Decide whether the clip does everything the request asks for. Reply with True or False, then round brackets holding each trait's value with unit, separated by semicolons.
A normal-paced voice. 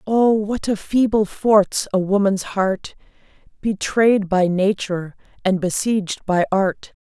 False (130 wpm)